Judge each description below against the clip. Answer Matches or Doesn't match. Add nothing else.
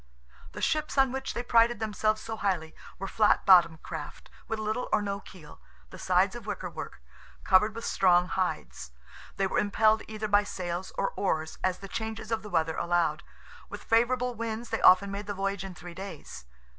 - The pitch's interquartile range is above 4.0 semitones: Doesn't match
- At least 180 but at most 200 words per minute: Matches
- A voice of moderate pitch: Doesn't match